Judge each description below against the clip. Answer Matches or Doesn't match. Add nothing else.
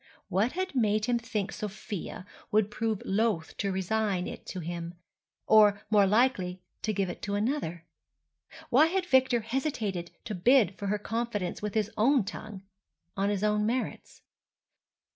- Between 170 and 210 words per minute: Doesn't match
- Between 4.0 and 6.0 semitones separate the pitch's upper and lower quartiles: Doesn't match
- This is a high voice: Matches